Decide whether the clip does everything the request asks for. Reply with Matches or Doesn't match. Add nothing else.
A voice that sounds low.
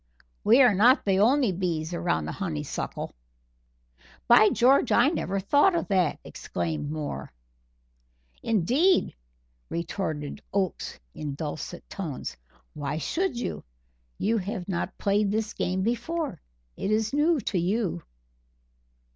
Doesn't match